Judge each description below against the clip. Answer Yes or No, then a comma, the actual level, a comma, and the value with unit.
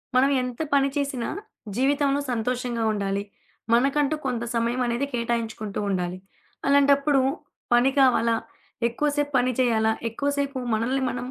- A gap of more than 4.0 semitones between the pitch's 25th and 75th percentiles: No, average, 3.1 semitones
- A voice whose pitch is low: No, very high, 250 Hz